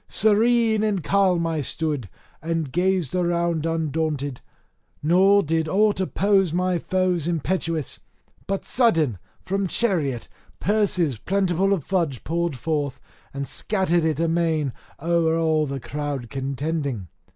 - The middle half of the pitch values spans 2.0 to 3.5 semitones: No, average, 4.0 semitones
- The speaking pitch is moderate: Yes, medium, 165 Hz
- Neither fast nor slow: No, slow, 125 wpm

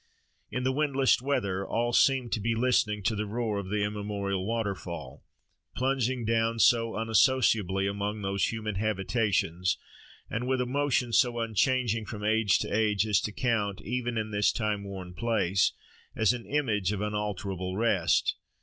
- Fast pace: No, average, 160 wpm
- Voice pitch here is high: No, low, 110 Hz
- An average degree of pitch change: Yes, average, 3.0 semitones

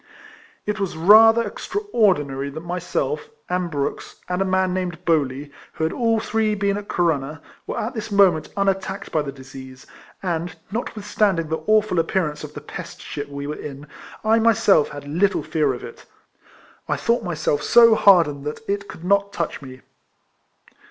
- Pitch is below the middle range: No, medium, 180 Hz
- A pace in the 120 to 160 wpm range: No, average, 170 wpm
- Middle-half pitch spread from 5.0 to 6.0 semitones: Yes, wide, 5.6 semitones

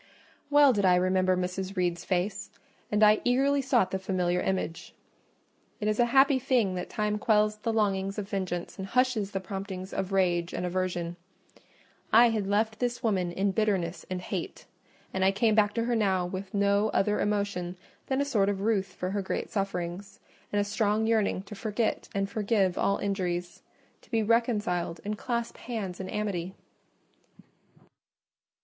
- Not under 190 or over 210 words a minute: No, average, 170 wpm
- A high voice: Yes, high, 200 Hz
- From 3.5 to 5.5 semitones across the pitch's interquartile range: No, average, 2.8 semitones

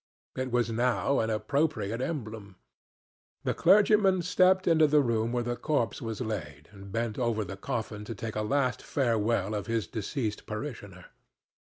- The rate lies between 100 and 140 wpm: No, average, 160 wpm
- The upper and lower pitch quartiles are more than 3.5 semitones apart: Yes, average, 4.7 semitones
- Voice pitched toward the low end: Yes, low, 115 Hz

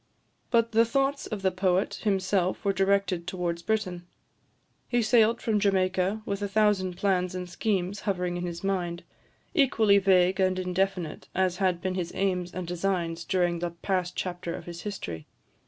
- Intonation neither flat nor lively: No, narrow, 2.1 semitones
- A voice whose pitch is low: No, medium, 185 Hz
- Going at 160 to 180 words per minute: Yes, average, 165 wpm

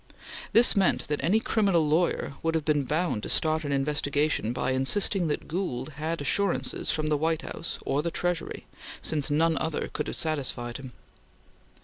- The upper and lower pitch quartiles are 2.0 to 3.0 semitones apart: Yes, average, 2.7 semitones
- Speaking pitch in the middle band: Yes, medium, 155 Hz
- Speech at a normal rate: Yes, average, 170 wpm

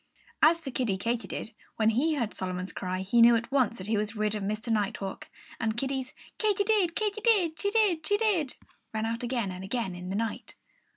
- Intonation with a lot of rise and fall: Yes, wide, 7.3 semitones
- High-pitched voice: Yes, high, 235 Hz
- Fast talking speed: Yes, fast, 210 wpm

